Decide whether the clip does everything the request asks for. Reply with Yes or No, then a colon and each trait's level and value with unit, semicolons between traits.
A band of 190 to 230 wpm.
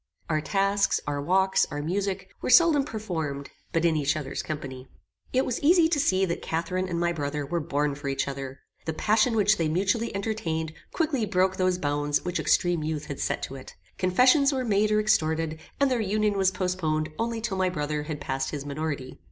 Yes: average, 200 wpm